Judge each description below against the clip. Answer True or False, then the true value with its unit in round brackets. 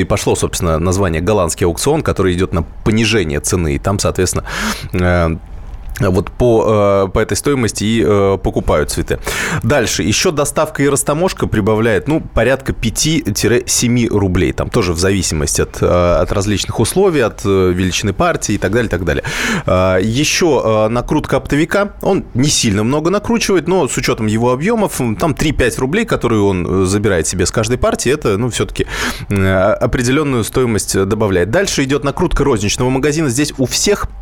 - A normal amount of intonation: False (6.3 semitones)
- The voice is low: True (110 Hz)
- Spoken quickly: False (150 wpm)